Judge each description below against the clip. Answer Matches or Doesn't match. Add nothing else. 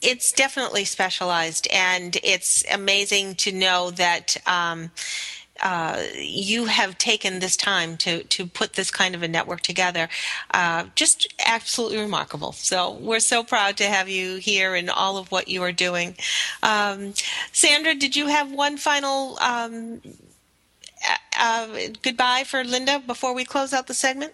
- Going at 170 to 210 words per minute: Doesn't match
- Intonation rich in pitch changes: Matches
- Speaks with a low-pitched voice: Doesn't match